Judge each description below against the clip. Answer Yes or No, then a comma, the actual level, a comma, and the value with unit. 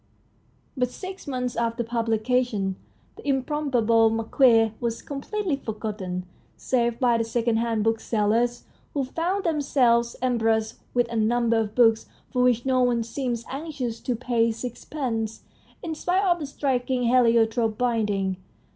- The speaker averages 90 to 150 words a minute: Yes, average, 145 wpm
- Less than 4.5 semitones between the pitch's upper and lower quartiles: Yes, narrow, 2.5 semitones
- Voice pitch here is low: No, high, 235 Hz